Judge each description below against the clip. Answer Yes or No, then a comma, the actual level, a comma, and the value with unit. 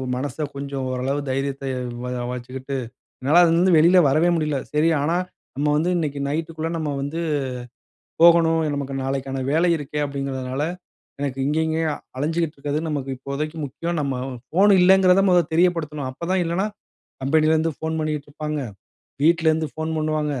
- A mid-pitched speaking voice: Yes, medium, 150 Hz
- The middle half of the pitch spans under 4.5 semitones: Yes, average, 3.0 semitones